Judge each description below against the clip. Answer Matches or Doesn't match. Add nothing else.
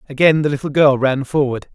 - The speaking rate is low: Doesn't match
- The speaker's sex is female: Doesn't match